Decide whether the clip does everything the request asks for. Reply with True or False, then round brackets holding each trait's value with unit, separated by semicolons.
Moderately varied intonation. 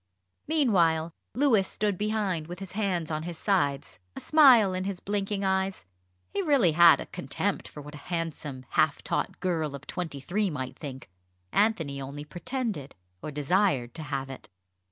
False (5.7 semitones)